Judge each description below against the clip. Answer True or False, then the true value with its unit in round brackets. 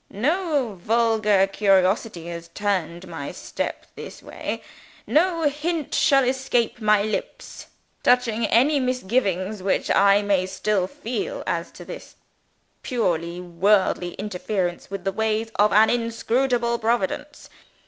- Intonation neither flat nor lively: True (4.7 semitones)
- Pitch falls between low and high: False (215 Hz)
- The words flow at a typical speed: False (120 wpm)